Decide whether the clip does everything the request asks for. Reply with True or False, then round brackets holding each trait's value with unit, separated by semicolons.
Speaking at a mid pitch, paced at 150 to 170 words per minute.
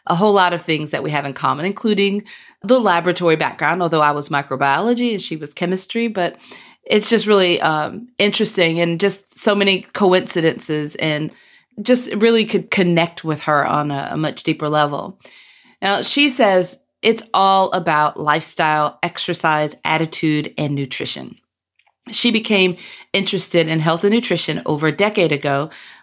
True (175 Hz; 155 wpm)